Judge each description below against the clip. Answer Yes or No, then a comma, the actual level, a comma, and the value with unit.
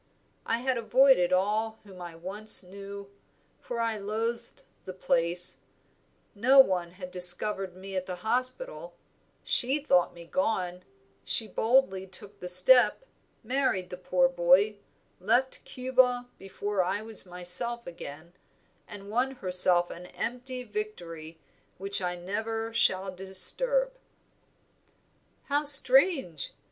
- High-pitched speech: Yes, high, 200 Hz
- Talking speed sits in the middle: No, slow, 120 wpm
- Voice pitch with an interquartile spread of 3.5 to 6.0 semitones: Yes, average, 5.1 semitones